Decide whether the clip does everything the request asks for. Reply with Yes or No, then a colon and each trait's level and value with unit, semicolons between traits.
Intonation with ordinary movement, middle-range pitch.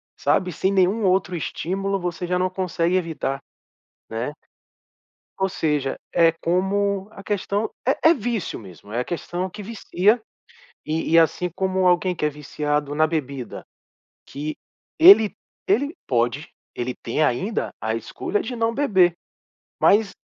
Yes: average, 4.8 semitones; medium, 180 Hz